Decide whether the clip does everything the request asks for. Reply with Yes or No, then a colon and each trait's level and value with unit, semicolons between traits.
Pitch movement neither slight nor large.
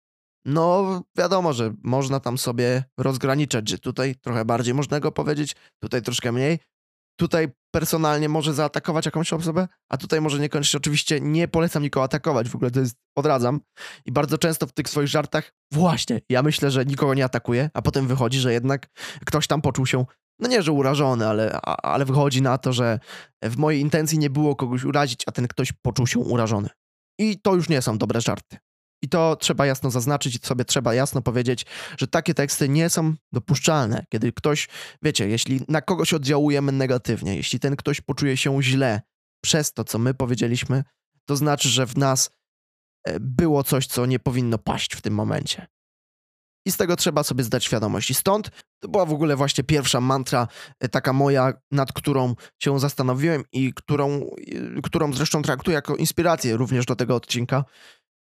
Yes: average, 3.3 semitones